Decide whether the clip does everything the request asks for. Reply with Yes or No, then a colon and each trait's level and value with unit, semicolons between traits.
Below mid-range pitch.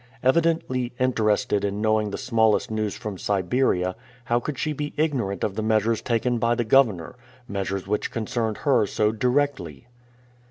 Yes: low, 110 Hz